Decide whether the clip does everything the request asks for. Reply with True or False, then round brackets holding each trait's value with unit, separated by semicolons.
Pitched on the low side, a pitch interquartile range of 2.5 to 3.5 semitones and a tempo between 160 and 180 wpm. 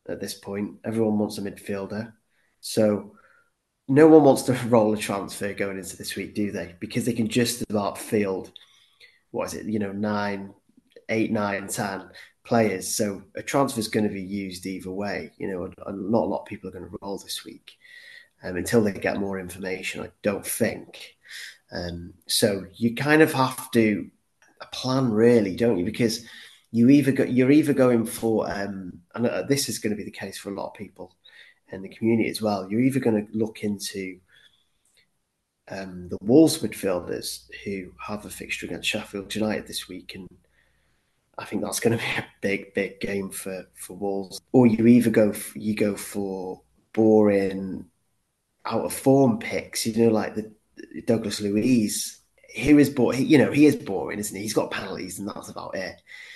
False (105 Hz; 3.2 semitones; 190 wpm)